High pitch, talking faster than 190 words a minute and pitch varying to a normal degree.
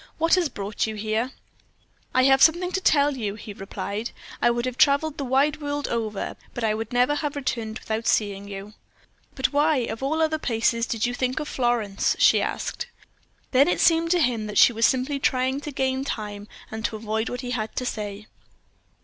Yes: high, 245 Hz; average, 200 wpm; average, 4.6 semitones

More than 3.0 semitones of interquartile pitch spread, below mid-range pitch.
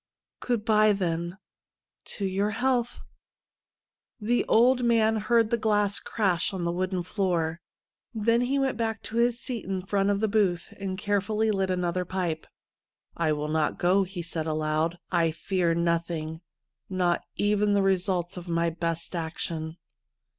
No: average, 4.1 semitones; high, 190 Hz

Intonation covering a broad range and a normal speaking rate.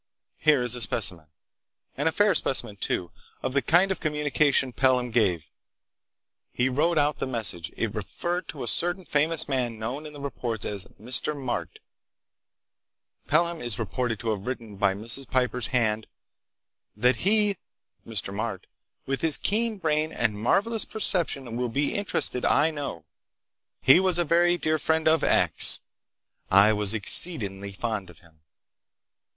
Yes: wide, 6.5 semitones; average, 150 wpm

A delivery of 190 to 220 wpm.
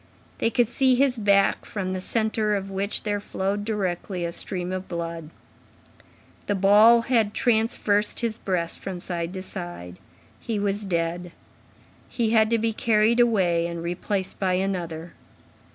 No: average, 150 wpm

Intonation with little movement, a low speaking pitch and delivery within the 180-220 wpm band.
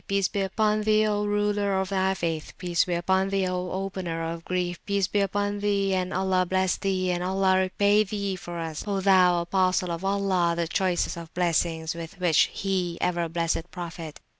No: narrow, 2.2 semitones; medium, 185 Hz; average, 190 wpm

